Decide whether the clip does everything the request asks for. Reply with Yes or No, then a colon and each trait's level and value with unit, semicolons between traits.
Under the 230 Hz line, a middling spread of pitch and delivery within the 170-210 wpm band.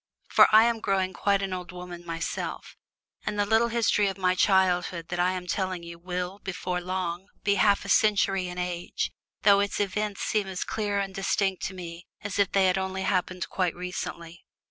No: high, 190 Hz; narrow, 2.0 semitones; average, 195 wpm